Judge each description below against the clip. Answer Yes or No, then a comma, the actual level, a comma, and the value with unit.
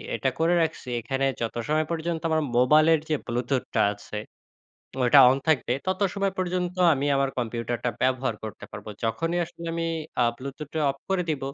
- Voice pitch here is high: No, medium, 145 Hz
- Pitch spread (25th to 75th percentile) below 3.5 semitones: No, average, 4.8 semitones